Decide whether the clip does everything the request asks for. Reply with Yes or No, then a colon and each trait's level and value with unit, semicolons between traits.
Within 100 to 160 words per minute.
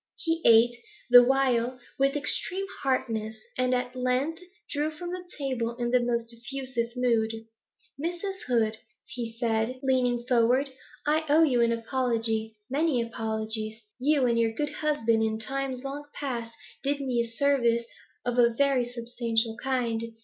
Yes: average, 150 wpm